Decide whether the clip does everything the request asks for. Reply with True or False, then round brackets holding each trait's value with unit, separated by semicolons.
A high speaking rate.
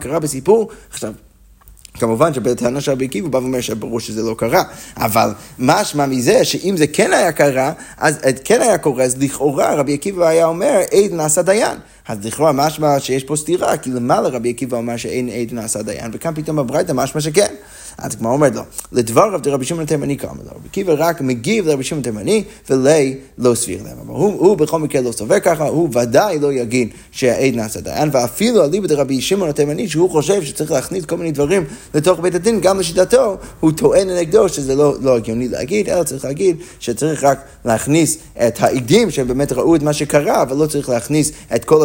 True (175 wpm)